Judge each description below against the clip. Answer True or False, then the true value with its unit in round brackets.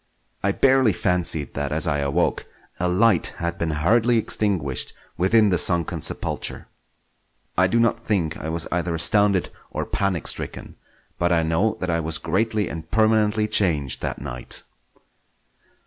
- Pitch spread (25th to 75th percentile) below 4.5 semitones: False (4.8 semitones)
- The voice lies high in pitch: False (90 Hz)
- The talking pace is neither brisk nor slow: True (150 wpm)